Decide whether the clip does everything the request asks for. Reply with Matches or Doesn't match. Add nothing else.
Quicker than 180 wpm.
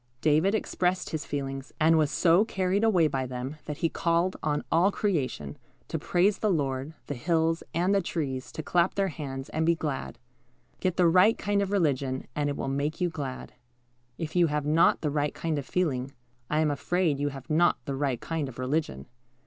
Matches